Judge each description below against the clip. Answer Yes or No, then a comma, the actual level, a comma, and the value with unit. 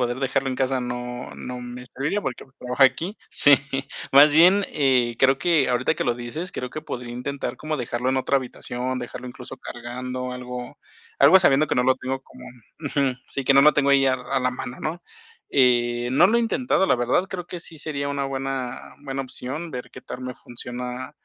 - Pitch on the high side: No, low, 130 Hz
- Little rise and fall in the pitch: Yes, narrow, 2.3 semitones